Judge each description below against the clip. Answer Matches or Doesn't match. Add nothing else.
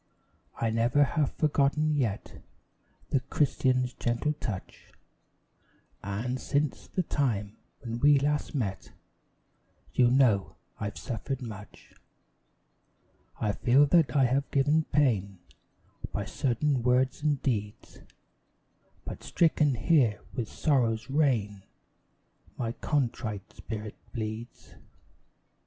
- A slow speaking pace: Matches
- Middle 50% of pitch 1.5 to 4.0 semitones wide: Doesn't match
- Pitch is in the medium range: Doesn't match